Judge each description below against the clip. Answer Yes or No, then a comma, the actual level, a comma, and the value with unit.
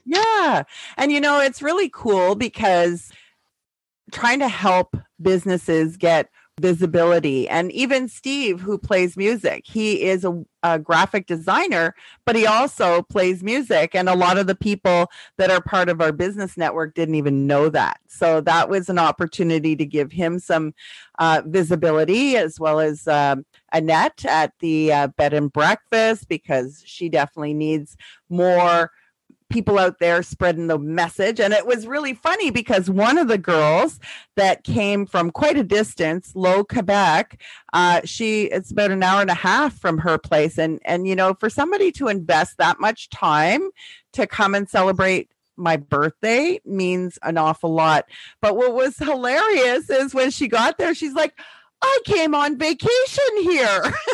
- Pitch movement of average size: No, wide, 6.3 semitones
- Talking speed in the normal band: Yes, average, 165 wpm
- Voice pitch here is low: No, medium, 185 Hz